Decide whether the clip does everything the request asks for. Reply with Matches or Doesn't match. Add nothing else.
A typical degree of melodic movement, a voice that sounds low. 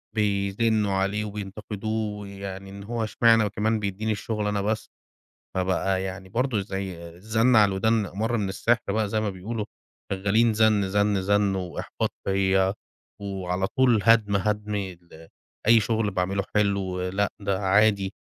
Doesn't match